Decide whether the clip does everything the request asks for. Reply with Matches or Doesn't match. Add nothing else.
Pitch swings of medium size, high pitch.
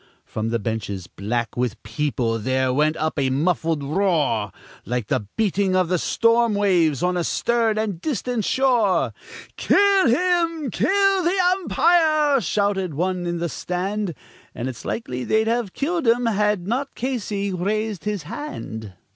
Doesn't match